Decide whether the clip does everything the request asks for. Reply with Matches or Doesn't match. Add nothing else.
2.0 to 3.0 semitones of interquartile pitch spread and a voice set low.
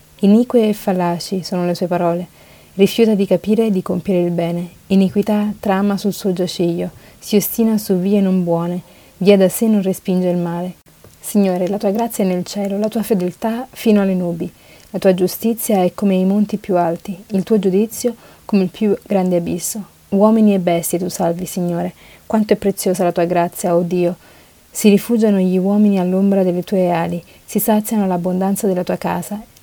Doesn't match